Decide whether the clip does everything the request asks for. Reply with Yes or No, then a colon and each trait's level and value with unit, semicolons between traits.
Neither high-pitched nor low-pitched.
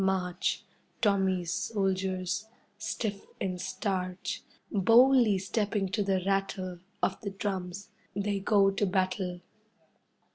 No: high, 195 Hz